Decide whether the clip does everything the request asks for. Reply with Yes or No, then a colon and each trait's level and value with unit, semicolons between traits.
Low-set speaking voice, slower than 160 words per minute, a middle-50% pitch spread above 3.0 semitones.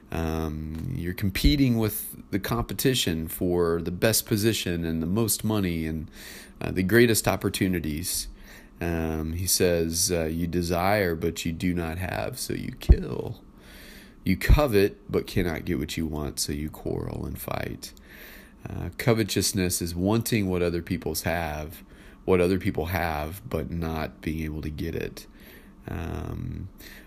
Yes: very low, 85 Hz; average, 145 wpm; average, 3.7 semitones